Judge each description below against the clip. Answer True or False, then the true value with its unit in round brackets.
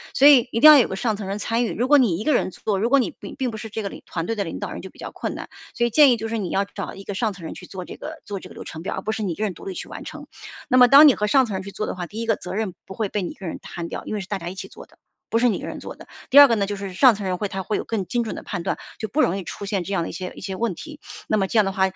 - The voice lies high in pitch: True (210 Hz)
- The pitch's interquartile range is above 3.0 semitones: True (3.6 semitones)